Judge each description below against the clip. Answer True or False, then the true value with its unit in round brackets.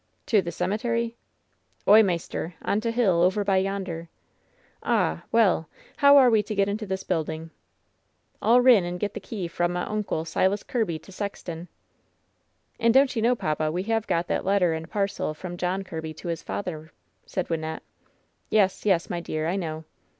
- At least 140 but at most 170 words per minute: False (195 wpm)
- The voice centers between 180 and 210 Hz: True (190 Hz)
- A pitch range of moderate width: True (4.1 semitones)